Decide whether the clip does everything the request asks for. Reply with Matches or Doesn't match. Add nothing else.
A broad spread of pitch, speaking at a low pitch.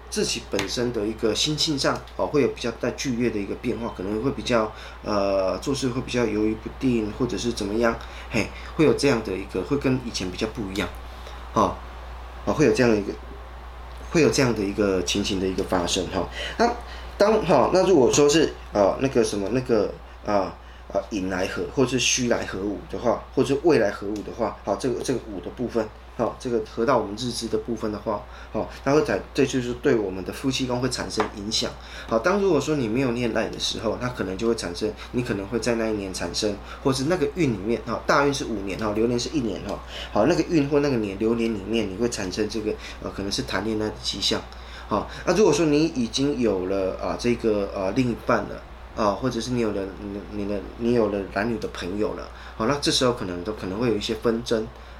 Doesn't match